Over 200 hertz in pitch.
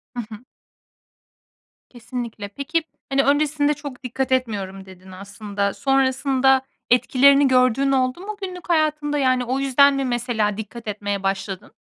Yes: very high, 255 Hz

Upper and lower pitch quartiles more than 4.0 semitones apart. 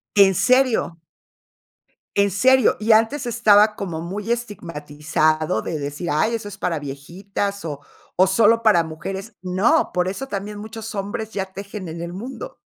Yes: average, 4.6 semitones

